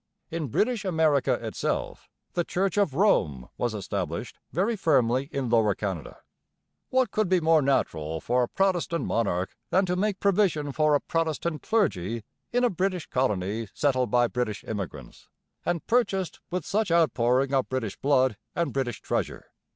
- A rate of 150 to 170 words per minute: Yes, average, 155 wpm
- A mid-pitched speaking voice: Yes, medium, 145 Hz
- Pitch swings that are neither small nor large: No, wide, 7.7 semitones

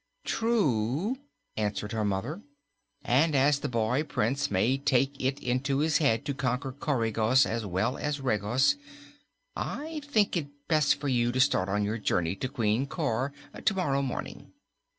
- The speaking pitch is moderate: No, low, 130 Hz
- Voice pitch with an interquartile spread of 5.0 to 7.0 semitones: No, average, 4.5 semitones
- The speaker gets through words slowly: No, average, 150 wpm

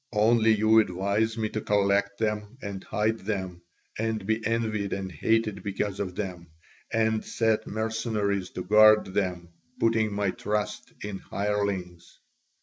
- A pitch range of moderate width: No, narrow, 2.0 semitones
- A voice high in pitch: No, low, 105 Hz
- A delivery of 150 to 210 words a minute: No, average, 140 wpm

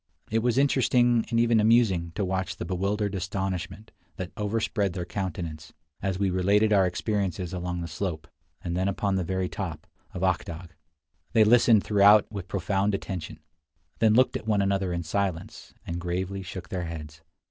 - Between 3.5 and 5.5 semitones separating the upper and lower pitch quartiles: No, average, 2.9 semitones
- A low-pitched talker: Yes, very low, 95 Hz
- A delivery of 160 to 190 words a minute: Yes, average, 170 wpm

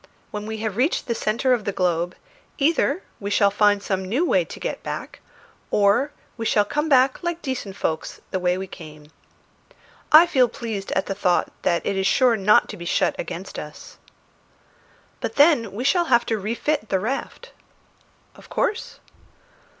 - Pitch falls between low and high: No, high, 215 Hz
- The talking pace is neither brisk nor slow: Yes, average, 175 wpm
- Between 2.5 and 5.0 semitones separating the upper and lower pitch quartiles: No, wide, 5.5 semitones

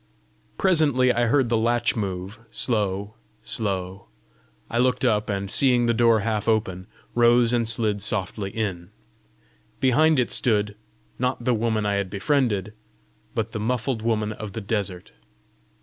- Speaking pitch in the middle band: No, low, 110 Hz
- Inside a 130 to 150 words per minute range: Yes, average, 145 wpm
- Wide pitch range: No, average, 3.0 semitones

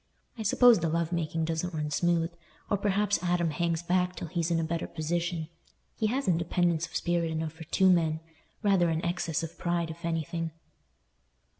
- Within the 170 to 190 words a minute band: Yes, average, 175 wpm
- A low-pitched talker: No, medium, 170 Hz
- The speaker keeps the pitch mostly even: Yes, narrow, 1.6 semitones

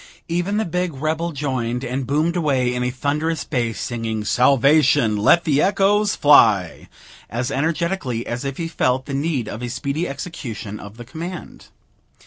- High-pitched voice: No, medium, 140 Hz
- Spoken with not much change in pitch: No, average, 5.1 semitones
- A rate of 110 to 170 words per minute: Yes, average, 160 wpm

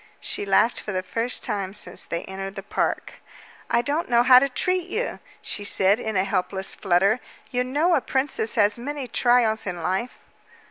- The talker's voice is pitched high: Yes, high, 220 Hz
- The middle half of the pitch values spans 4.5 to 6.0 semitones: Yes, average, 4.8 semitones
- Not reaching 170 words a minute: No, average, 185 wpm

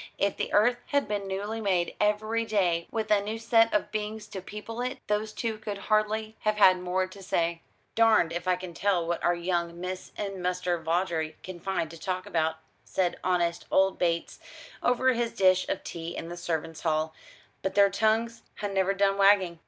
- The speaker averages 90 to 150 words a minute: No, average, 195 wpm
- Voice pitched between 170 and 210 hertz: Yes, high, 190 Hz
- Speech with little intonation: No, average, 3.5 semitones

